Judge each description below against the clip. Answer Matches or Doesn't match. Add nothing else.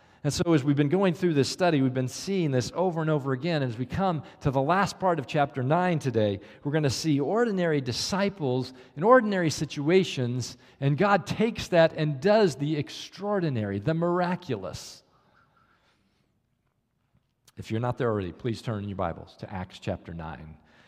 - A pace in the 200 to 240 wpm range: Doesn't match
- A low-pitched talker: Doesn't match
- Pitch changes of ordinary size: Doesn't match